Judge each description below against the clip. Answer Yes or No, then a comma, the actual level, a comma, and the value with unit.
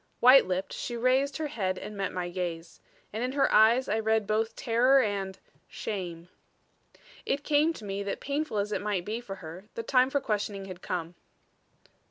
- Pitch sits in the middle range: No, high, 215 Hz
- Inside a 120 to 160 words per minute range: No, average, 190 wpm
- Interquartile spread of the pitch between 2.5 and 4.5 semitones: No, average, 4.9 semitones